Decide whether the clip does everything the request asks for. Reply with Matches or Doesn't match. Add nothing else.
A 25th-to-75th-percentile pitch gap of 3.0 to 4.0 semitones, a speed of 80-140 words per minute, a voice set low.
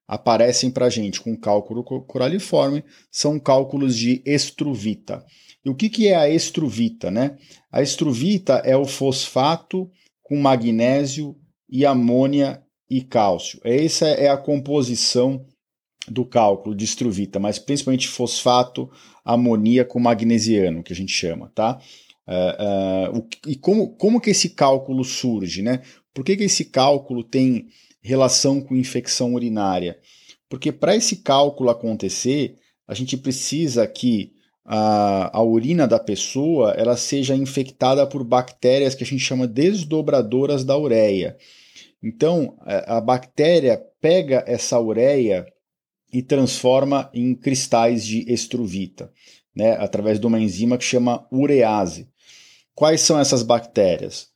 Matches